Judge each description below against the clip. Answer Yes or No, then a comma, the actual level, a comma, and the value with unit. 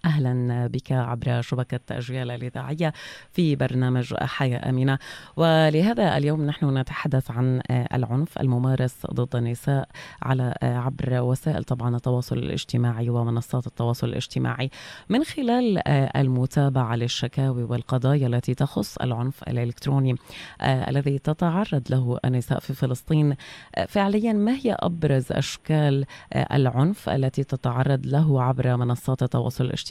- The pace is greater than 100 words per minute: Yes, average, 110 wpm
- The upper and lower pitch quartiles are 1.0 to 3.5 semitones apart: Yes, average, 2.7 semitones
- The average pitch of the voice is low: Yes, low, 130 Hz